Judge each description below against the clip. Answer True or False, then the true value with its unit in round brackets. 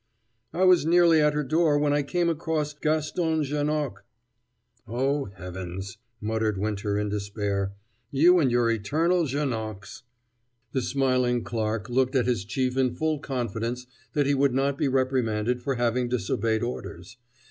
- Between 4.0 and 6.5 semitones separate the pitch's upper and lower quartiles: True (4.9 semitones)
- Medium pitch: False (125 Hz)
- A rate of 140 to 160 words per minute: True (155 wpm)